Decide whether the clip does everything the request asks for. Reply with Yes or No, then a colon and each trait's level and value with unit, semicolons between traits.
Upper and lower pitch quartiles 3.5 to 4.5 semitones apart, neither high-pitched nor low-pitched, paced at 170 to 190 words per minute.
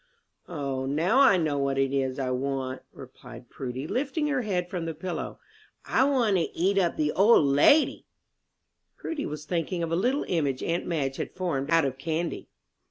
No: wide, 5.4 semitones; medium, 160 Hz; average, 180 wpm